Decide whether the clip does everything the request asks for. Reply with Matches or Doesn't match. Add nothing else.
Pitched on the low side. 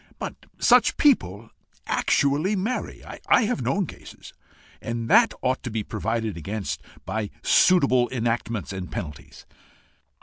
Matches